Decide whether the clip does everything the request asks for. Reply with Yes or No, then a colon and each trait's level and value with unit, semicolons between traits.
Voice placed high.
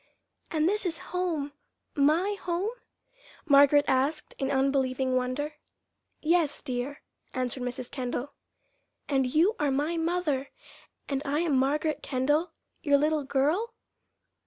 Yes: very high, 290 Hz